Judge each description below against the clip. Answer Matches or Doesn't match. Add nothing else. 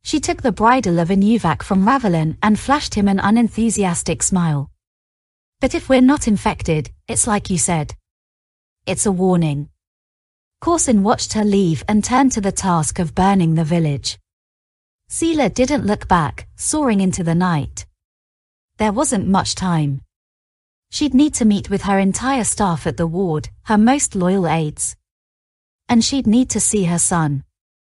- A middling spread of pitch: Doesn't match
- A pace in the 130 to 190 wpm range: Matches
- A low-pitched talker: Doesn't match